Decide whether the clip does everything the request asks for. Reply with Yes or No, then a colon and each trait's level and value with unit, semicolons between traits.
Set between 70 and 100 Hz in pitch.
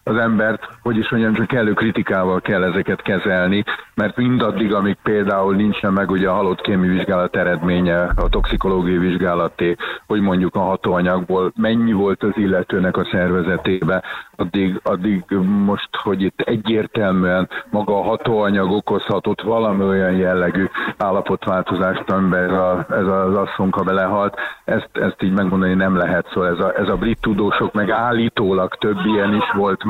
Yes: very low, 95 Hz